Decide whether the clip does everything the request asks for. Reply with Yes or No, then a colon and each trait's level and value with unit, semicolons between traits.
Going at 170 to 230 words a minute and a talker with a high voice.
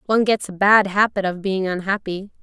Yes: average, 200 wpm; high, 195 Hz